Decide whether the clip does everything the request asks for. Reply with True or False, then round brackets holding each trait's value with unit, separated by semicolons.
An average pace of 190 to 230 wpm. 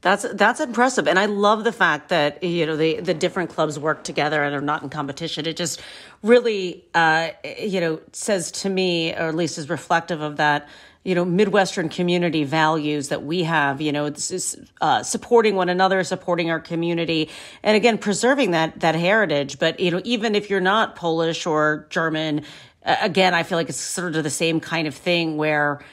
True (200 wpm)